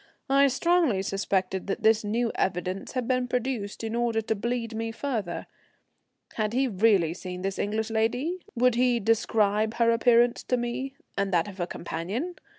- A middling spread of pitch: Yes, average, 3.7 semitones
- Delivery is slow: No, average, 165 wpm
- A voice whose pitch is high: Yes, high, 225 Hz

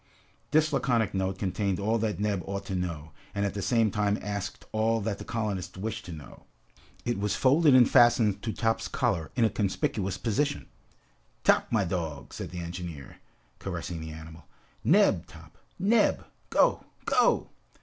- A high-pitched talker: No, low, 100 Hz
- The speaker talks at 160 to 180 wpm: Yes, average, 165 wpm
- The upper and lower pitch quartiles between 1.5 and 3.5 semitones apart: No, average, 3.9 semitones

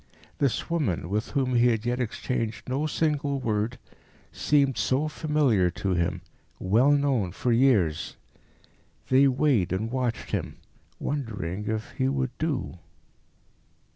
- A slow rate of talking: Yes, slow, 130 wpm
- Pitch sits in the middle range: No, low, 125 Hz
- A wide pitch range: No, average, 4.7 semitones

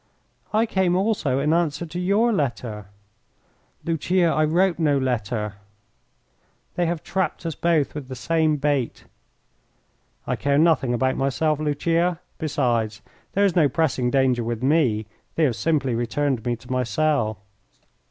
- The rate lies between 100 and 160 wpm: Yes, average, 145 wpm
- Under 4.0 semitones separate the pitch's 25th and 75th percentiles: No, average, 4.9 semitones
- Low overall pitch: No, medium, 145 Hz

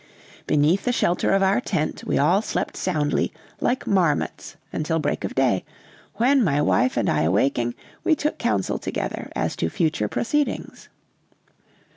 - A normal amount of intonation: No, wide, 7.0 semitones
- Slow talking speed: No, average, 150 wpm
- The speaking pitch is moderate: Yes, medium, 155 Hz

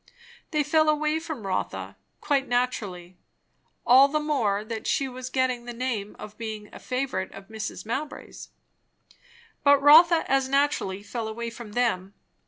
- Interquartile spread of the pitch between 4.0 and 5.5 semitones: Yes, average, 4.8 semitones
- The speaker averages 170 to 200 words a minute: No, average, 150 wpm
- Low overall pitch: No, very high, 250 Hz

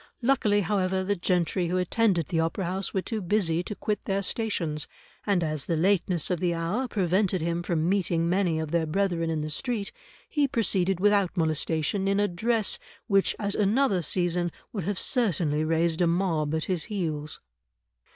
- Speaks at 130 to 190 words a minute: Yes, average, 180 wpm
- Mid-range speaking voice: Yes, medium, 180 Hz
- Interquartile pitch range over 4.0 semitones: No, average, 3.4 semitones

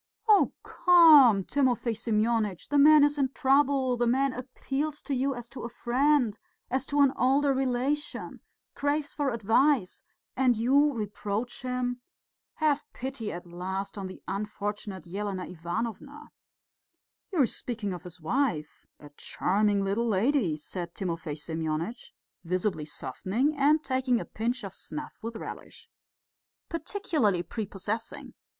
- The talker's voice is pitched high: Yes, high, 235 Hz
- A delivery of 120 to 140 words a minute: Yes, slow, 135 wpm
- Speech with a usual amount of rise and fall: No, wide, 5.9 semitones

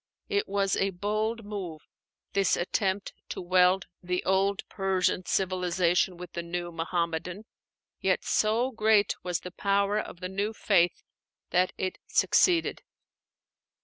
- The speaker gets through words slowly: Yes, slow, 130 wpm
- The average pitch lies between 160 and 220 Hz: Yes, high, 190 Hz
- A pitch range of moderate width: No, narrow, 2.3 semitones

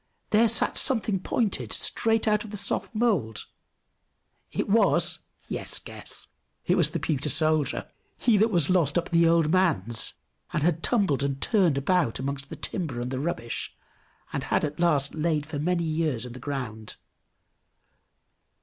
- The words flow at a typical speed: Yes, average, 165 wpm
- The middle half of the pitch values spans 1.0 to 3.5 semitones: No, wide, 5.4 semitones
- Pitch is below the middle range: No, medium, 160 Hz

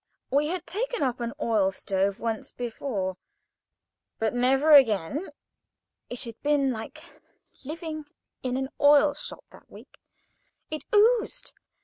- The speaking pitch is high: Yes, very high, 270 Hz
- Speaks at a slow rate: Yes, slow, 120 wpm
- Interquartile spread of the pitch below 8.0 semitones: Yes, average, 5.1 semitones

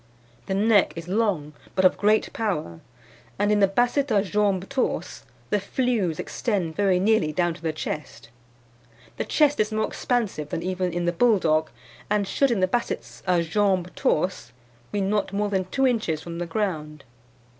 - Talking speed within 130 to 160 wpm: No, average, 175 wpm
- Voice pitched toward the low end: No, high, 195 Hz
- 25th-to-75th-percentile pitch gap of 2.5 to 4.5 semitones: Yes, average, 4.0 semitones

